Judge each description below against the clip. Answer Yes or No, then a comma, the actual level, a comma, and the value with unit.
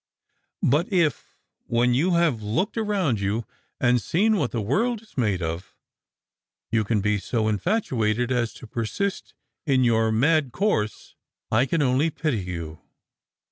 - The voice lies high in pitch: No, low, 125 Hz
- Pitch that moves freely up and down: Yes, wide, 7.2 semitones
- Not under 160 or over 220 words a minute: No, average, 150 wpm